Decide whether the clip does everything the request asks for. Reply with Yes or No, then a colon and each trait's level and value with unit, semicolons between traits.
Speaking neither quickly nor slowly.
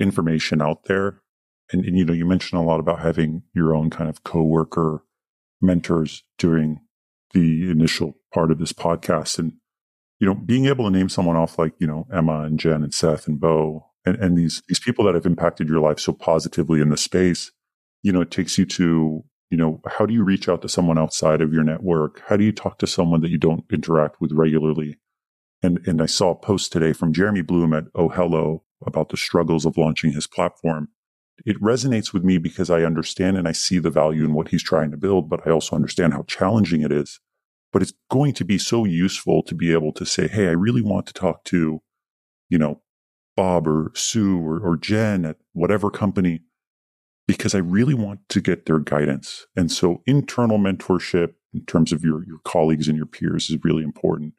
No: fast, 210 wpm